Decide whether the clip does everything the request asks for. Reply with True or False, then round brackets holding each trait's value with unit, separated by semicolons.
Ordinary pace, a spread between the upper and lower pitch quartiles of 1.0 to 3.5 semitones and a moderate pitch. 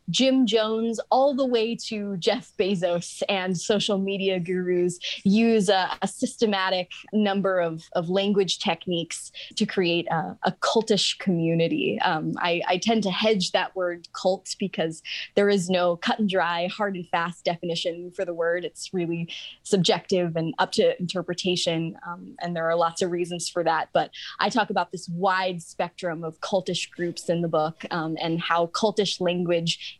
True (170 wpm; 2.9 semitones; 180 Hz)